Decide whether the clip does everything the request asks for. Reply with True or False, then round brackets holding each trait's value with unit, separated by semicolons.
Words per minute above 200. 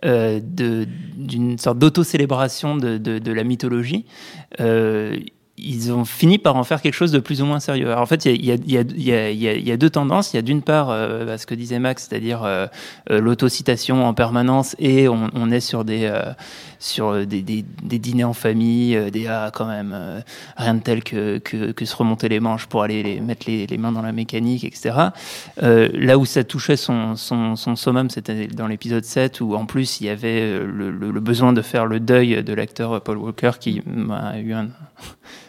True (220 wpm)